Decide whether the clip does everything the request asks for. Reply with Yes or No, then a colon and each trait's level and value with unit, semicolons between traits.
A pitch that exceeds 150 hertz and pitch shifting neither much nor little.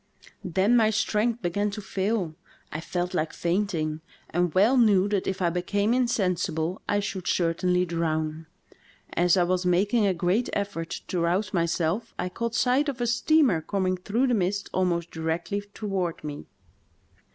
Yes: medium, 185 Hz; average, 3.5 semitones